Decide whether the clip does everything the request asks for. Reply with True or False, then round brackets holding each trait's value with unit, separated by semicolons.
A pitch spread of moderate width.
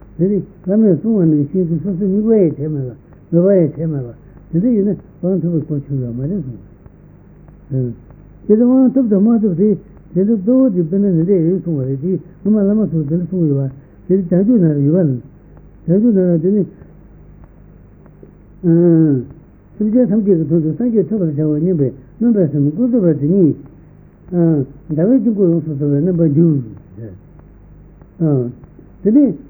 True (4.8 semitones)